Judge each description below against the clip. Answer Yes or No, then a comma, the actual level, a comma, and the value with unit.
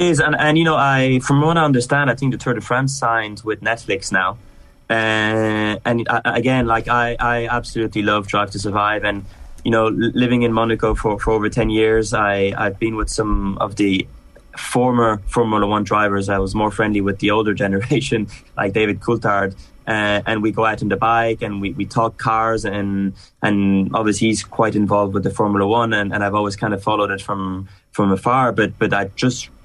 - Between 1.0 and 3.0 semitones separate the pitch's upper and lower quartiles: Yes, narrow, 2.5 semitones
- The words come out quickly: Yes, fast, 210 wpm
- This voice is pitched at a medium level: No, low, 110 Hz